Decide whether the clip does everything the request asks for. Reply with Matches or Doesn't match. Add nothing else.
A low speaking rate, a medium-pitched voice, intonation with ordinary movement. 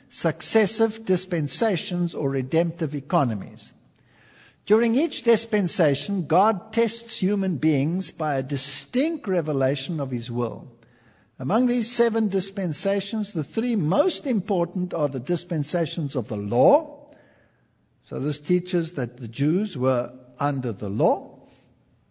Doesn't match